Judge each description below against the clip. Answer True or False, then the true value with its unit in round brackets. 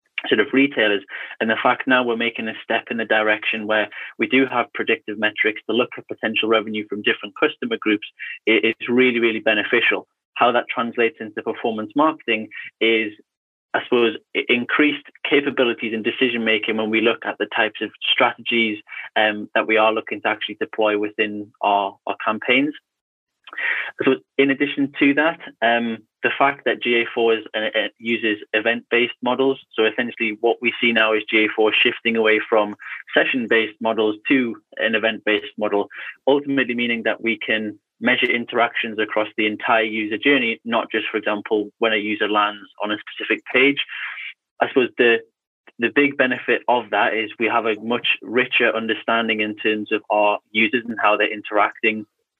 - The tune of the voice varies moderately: False (2.1 semitones)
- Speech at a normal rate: True (170 wpm)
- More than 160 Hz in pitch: False (115 Hz)